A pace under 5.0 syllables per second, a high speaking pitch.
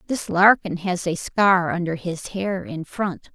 No: 3.8 syllables/s; medium, 180 Hz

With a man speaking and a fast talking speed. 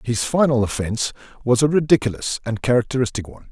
No: male; average, 155 wpm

